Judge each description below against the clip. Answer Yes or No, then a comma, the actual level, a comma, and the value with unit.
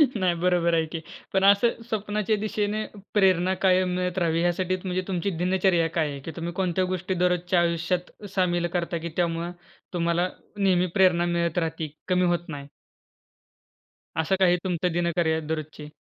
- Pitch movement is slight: Yes, narrow, 1.7 semitones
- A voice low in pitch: No, medium, 175 Hz